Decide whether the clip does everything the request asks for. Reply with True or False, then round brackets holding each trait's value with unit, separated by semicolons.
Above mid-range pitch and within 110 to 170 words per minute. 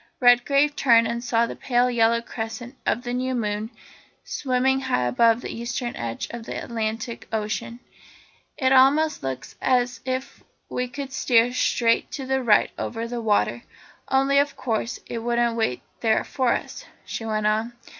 True (240 Hz; 165 wpm)